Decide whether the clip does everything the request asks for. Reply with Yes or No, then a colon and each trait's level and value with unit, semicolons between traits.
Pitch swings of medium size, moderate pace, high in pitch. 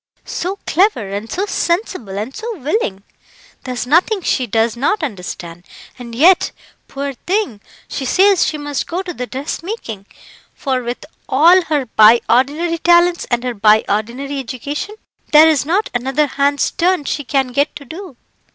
No: wide, 6.3 semitones; average, 160 wpm; very high, 280 Hz